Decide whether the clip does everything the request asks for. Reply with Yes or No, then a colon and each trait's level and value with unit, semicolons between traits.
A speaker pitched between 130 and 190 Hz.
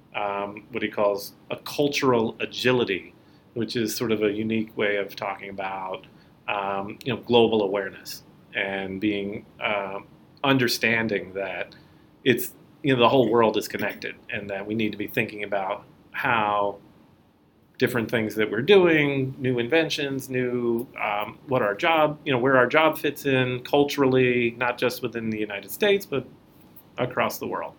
No: low, 115 Hz